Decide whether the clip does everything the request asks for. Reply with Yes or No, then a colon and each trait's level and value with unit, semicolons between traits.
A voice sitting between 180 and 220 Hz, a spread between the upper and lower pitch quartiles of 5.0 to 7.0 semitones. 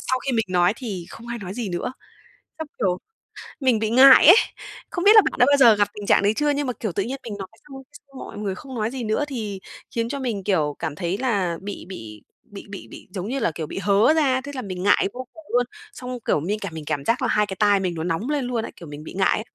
Yes: high, 215 Hz; wide, 5.5 semitones